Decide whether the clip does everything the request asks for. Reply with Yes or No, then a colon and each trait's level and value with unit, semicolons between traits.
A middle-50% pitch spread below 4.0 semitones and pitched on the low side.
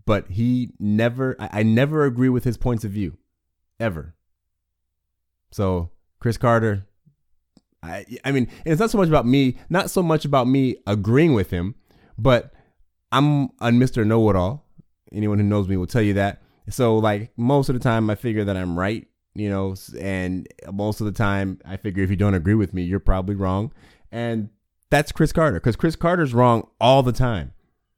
No: average, 4.8 semitones; low, 110 Hz